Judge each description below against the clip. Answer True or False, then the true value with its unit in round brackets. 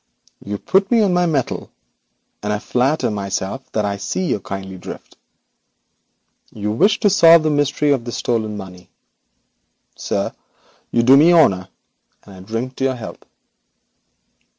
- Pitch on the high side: False (120 Hz)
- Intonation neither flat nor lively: False (7.3 semitones)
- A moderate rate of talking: True (155 wpm)